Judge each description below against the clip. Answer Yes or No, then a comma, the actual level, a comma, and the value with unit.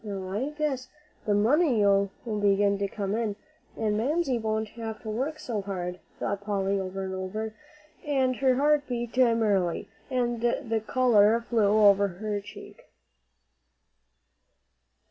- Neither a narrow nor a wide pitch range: Yes, average, 3.5 semitones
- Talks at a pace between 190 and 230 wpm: No, slow, 135 wpm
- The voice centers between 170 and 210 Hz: No, high, 220 Hz